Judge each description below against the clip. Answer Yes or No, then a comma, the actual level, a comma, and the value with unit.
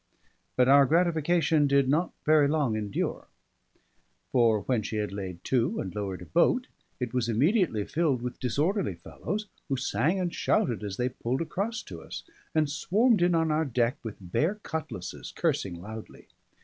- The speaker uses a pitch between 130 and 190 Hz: Yes, low, 135 Hz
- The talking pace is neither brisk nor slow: Yes, average, 165 wpm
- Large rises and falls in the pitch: Yes, wide, 7.1 semitones